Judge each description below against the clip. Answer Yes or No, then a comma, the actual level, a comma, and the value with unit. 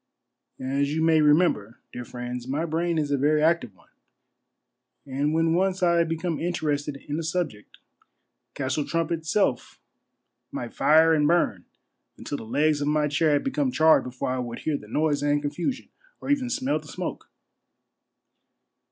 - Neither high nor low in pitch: Yes, medium, 155 Hz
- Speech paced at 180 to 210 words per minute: No, average, 165 wpm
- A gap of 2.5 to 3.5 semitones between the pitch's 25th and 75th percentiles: Yes, average, 2.8 semitones